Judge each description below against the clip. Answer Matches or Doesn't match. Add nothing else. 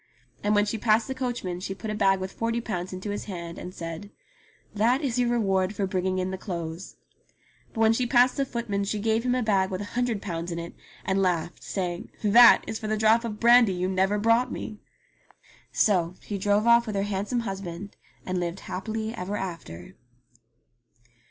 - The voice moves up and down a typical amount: Matches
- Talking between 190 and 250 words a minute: Matches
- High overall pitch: Matches